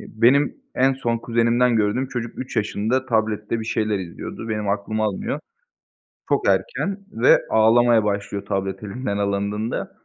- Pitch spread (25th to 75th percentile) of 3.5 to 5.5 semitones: No, average, 2.8 semitones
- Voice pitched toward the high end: No, low, 110 Hz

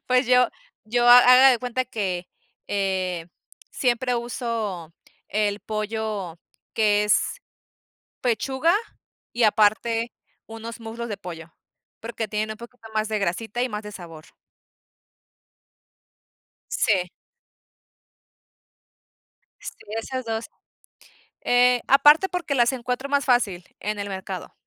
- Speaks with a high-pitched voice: Yes, high, 225 Hz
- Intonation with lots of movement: No, average, 3.3 semitones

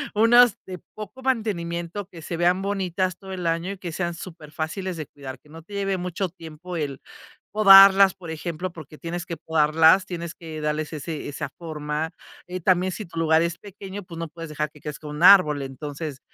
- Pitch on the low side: No, medium, 170 Hz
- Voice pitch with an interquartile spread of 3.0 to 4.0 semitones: Yes, average, 3.3 semitones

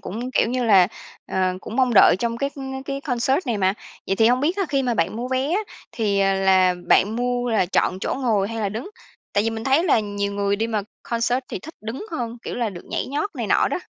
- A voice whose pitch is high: Yes, high, 230 Hz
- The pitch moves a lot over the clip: No, average, 4.3 semitones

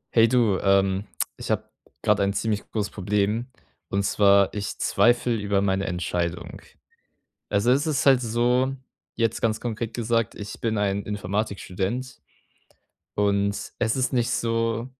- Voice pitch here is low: Yes, low, 105 Hz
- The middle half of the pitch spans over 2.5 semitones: Yes, average, 2.9 semitones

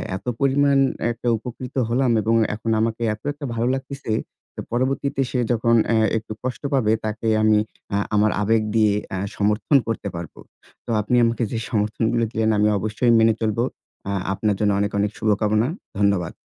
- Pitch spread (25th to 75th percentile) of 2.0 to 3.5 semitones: Yes, narrow, 2.4 semitones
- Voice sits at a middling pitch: No, low, 110 Hz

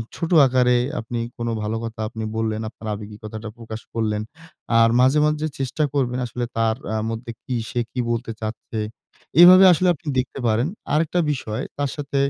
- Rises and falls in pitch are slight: No, average, 3.8 semitones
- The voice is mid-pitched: No, low, 120 Hz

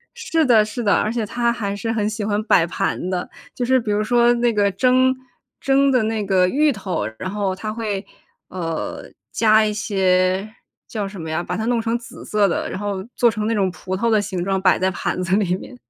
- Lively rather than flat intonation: No, average, 3.5 semitones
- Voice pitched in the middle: No, high, 210 Hz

